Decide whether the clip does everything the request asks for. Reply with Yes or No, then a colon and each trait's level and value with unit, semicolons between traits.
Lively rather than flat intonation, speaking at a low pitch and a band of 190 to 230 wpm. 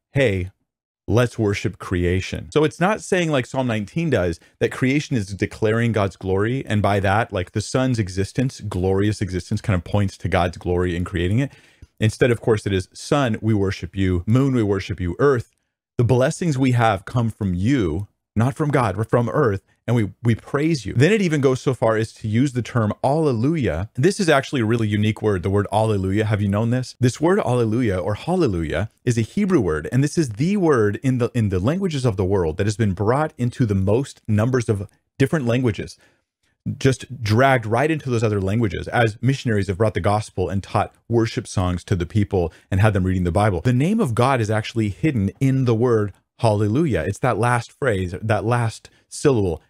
No: average, 4.3 semitones; low, 110 Hz; fast, 205 wpm